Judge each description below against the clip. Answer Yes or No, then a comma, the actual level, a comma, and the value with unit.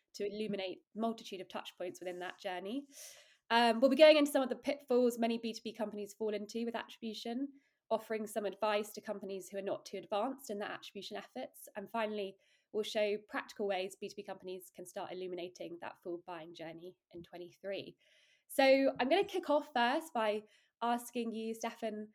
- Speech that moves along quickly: No, average, 180 wpm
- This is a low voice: No, high, 215 Hz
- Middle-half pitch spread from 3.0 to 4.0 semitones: Yes, average, 3.5 semitones